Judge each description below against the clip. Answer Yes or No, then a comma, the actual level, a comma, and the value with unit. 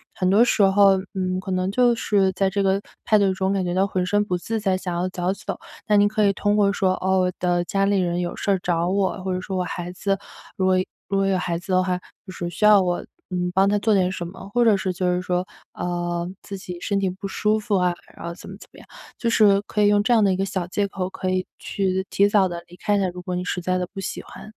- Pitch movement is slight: Yes, narrow, 1.8 semitones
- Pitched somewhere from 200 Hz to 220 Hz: No, high, 190 Hz